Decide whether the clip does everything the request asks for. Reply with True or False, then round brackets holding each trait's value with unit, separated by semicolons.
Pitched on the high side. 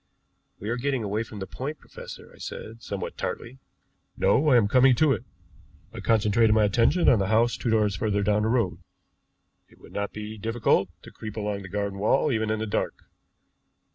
False (110 Hz)